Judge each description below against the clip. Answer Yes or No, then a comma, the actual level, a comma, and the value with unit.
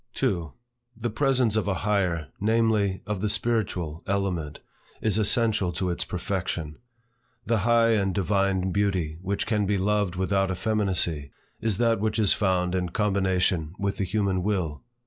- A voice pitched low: Yes, low, 100 Hz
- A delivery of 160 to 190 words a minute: No, average, 150 wpm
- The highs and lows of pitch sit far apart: No, average, 2.7 semitones